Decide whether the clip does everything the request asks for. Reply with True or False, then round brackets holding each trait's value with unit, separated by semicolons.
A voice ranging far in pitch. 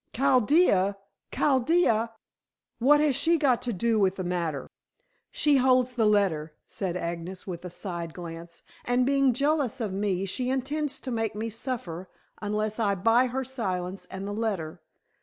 True (5.8 semitones)